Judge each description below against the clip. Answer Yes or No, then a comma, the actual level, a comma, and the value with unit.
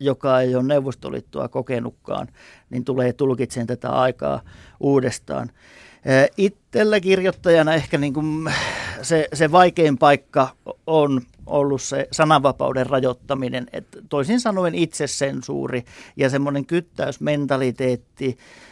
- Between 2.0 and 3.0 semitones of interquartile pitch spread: No, average, 3.7 semitones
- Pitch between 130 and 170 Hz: Yes, medium, 140 Hz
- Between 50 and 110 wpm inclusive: Yes, average, 105 wpm